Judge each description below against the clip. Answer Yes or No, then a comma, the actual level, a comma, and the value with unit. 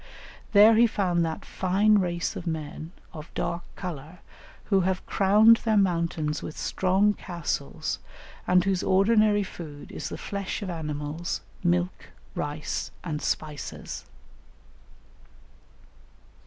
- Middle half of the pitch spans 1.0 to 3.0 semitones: No, average, 3.7 semitones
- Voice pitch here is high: No, medium, 180 Hz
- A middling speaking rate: No, slow, 115 wpm